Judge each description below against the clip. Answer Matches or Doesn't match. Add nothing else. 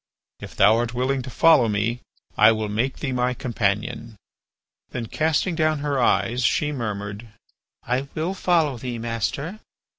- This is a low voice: Matches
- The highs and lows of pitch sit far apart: Doesn't match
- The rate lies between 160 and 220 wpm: Doesn't match